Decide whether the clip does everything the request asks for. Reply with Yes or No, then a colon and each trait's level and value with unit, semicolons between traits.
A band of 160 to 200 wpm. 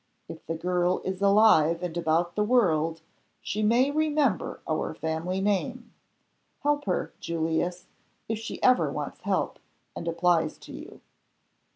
No: average, 140 wpm